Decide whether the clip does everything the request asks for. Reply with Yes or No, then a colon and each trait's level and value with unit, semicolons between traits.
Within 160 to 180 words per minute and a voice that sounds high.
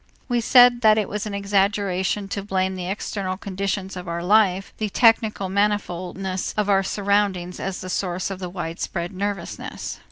Yes: average, 165 wpm; high, 195 Hz